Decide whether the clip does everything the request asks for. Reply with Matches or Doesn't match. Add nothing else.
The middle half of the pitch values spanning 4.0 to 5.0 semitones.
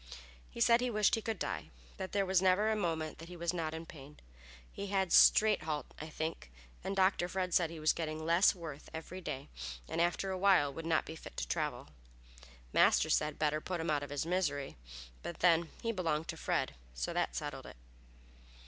Doesn't match